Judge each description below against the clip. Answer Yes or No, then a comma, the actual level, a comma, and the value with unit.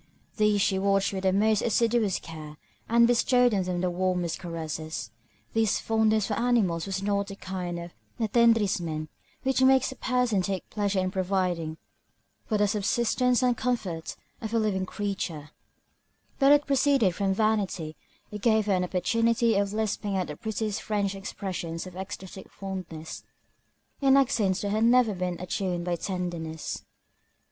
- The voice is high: Yes, high, 200 Hz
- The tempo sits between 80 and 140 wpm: No, average, 155 wpm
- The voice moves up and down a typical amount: Yes, average, 3.6 semitones